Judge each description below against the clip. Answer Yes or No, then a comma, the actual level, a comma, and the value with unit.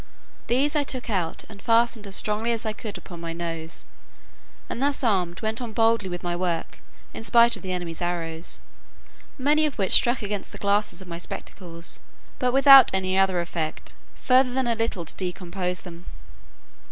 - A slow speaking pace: No, average, 180 wpm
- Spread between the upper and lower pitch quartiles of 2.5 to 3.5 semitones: No, average, 5.2 semitones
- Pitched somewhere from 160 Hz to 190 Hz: No, high, 200 Hz